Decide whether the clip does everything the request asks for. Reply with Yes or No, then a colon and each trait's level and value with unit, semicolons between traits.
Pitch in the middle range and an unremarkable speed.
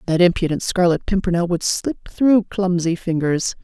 Yes: medium, 180 Hz; average, 150 wpm